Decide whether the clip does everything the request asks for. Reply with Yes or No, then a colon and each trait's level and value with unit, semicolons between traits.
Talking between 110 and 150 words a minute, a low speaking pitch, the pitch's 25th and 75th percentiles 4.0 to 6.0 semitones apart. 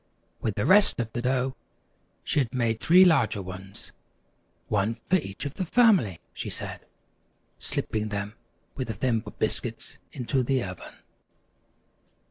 Yes: average, 140 wpm; low, 120 Hz; average, 5.1 semitones